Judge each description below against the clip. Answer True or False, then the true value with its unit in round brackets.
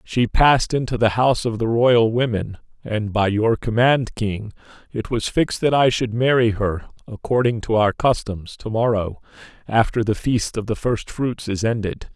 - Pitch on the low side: True (115 Hz)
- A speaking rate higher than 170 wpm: True (185 wpm)